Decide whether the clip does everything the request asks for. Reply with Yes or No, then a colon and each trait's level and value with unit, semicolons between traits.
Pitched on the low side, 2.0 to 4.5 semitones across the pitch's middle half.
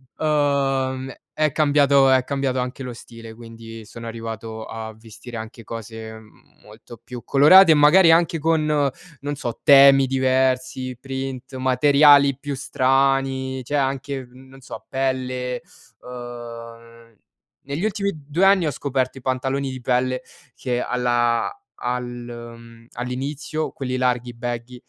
Yes: low, 130 Hz; narrow, 2.6 semitones